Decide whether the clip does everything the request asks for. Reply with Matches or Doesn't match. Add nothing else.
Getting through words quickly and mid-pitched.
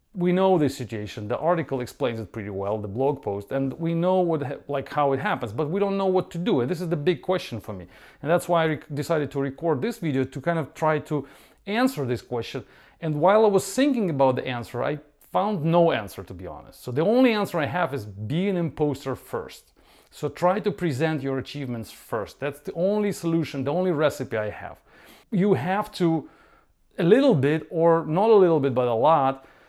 Matches